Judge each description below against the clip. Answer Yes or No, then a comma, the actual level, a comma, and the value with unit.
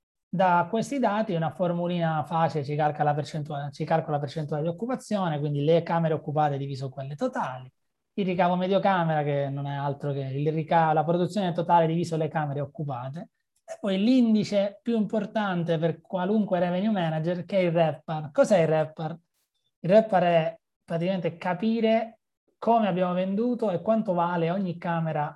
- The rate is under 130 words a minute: No, average, 165 wpm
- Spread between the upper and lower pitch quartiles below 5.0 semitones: Yes, average, 4.1 semitones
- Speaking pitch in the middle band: Yes, medium, 170 Hz